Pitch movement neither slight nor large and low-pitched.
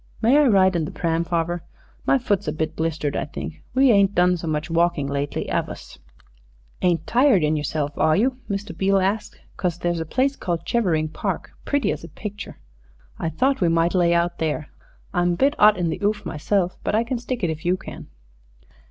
No: average, 4.4 semitones; medium, 175 Hz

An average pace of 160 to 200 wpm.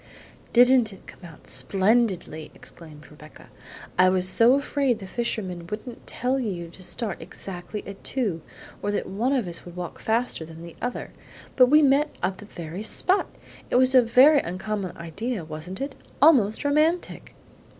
Yes: average, 165 wpm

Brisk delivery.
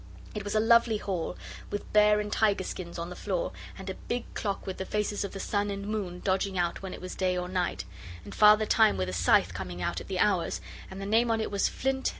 Yes: fast, 250 wpm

